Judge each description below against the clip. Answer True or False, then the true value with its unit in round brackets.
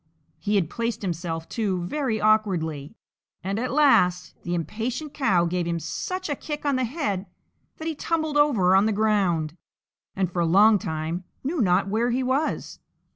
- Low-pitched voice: False (210 Hz)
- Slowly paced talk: False (175 wpm)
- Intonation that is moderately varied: False (6.6 semitones)